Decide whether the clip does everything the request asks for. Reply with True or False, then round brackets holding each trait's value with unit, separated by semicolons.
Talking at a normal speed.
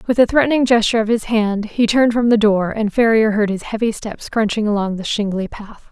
False (235 wpm)